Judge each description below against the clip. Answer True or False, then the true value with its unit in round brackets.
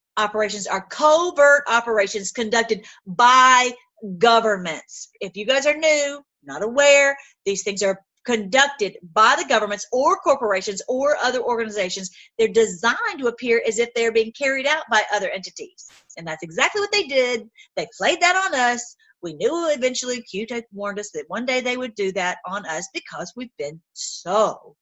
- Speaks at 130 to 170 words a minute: True (165 wpm)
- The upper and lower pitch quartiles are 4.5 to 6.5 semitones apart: True (5.5 semitones)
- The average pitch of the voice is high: True (235 Hz)